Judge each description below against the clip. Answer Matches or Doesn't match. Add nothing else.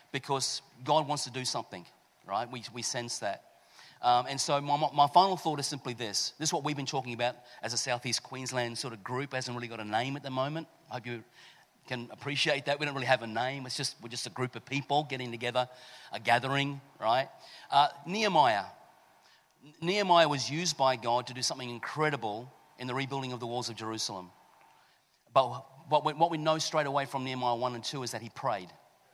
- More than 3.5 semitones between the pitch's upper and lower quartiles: Doesn't match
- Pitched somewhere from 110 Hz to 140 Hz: Matches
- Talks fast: Matches